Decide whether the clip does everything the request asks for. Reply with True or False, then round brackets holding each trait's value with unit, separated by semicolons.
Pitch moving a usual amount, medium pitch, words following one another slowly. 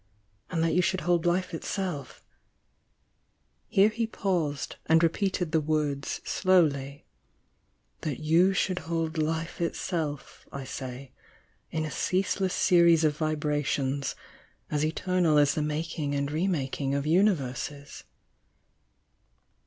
True (3.6 semitones; 155 Hz; 130 wpm)